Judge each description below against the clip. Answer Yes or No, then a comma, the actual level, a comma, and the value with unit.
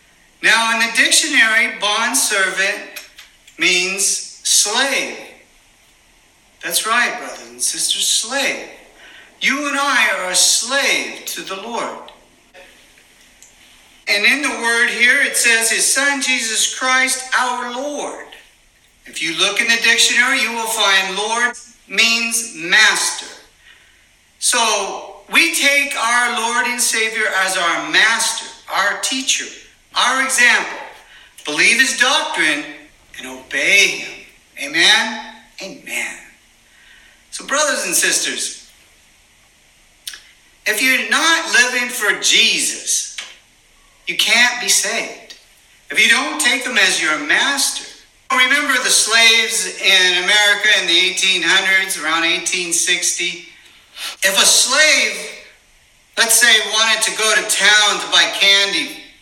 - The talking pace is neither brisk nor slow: No, slow, 115 wpm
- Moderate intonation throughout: Yes, average, 5.0 semitones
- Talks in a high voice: Yes, high, 225 Hz